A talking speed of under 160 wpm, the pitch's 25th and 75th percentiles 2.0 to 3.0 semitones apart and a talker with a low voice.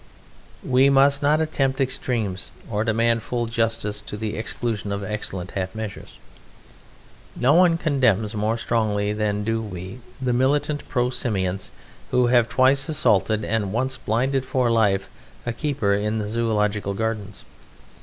No: average, 145 wpm; average, 3.7 semitones; low, 115 Hz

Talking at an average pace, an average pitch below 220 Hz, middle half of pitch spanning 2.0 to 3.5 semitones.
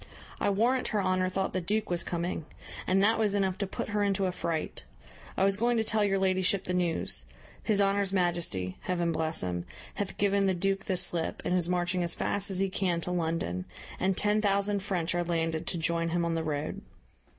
No: fast, 215 wpm; medium, 185 Hz; average, 2.8 semitones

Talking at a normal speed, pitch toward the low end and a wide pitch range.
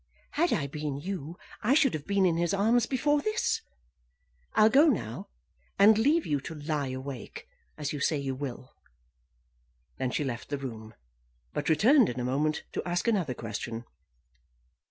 No: average, 165 wpm; medium, 155 Hz; wide, 8.1 semitones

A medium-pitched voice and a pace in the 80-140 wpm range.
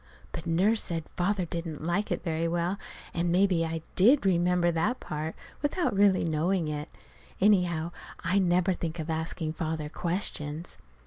No: medium, 170 Hz; average, 150 wpm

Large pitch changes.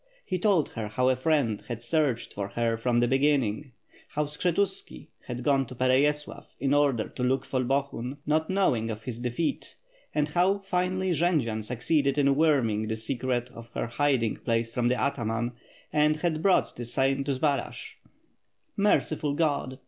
No: average, 4.2 semitones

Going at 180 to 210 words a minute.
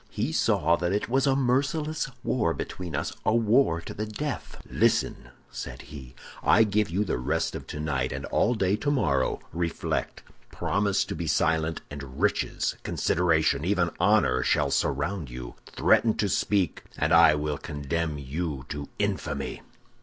No: average, 155 wpm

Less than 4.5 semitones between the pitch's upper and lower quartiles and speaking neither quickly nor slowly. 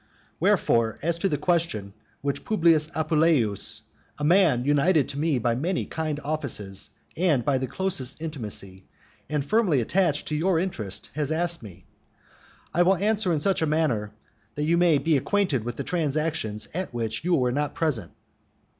No: wide, 5.5 semitones; average, 165 wpm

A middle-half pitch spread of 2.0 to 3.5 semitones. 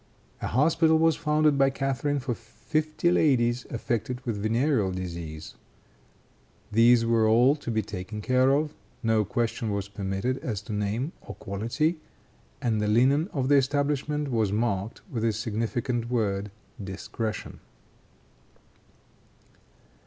No: average, 4.4 semitones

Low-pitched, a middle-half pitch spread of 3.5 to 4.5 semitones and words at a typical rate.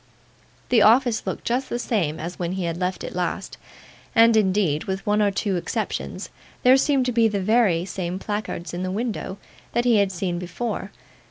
No: high, 200 Hz; average, 4.2 semitones; average, 190 wpm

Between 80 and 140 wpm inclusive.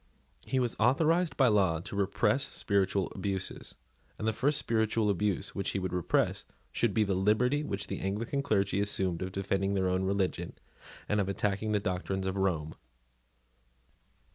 No: average, 165 wpm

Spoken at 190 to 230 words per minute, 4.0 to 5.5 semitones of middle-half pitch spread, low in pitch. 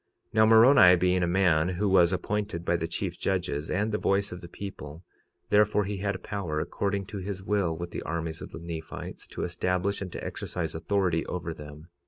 No: fast, 205 wpm; average, 3.1 semitones; very low, 90 Hz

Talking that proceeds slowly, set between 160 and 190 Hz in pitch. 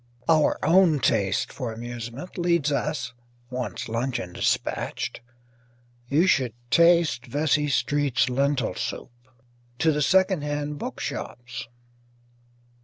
No: slow, 105 wpm; medium, 145 Hz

